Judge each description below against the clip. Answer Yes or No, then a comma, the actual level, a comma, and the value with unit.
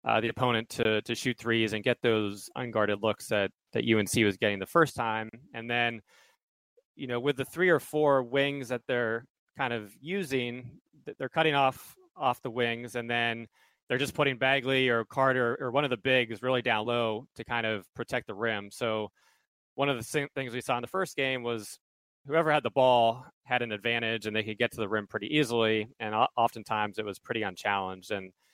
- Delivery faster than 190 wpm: Yes, fast, 205 wpm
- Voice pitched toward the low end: Yes, low, 120 Hz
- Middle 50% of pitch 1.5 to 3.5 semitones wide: Yes, average, 3.2 semitones